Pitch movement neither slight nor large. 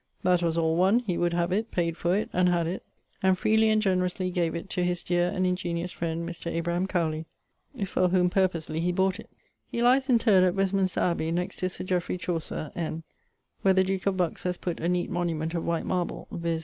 No: narrow, 1.9 semitones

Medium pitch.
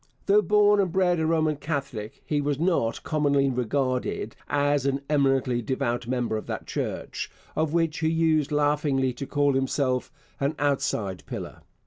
Yes: medium, 145 Hz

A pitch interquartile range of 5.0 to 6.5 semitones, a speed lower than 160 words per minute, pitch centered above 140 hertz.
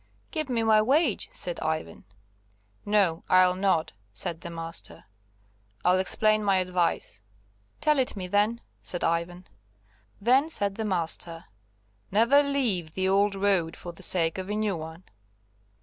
No: average, 4.1 semitones; average, 145 wpm; high, 190 Hz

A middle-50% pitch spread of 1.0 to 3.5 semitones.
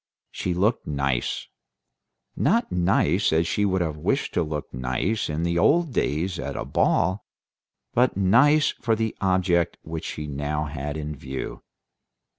No: average, 5.3 semitones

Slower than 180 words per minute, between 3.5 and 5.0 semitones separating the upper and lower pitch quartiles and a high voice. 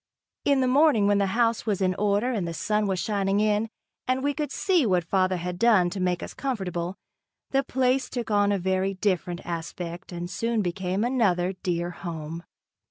No: average, 190 wpm; average, 4.5 semitones; high, 195 Hz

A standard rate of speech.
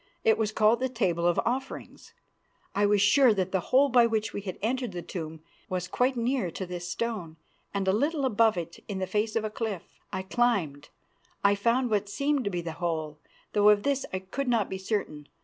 No: fast, 215 wpm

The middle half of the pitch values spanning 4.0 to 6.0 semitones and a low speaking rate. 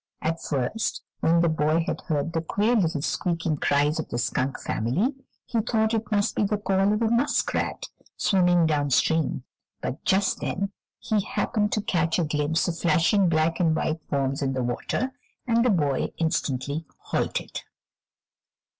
No: wide, 5.5 semitones; average, 165 wpm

